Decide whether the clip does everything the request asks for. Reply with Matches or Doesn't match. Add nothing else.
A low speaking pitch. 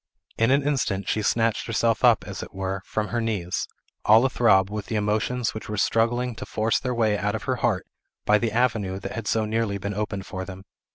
Matches